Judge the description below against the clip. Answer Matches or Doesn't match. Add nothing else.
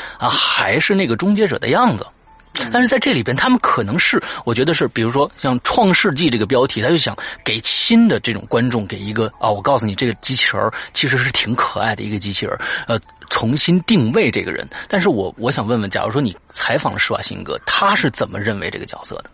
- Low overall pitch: Matches